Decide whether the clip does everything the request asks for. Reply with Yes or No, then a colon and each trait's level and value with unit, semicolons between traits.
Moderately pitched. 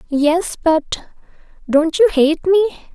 No: very high, 330 Hz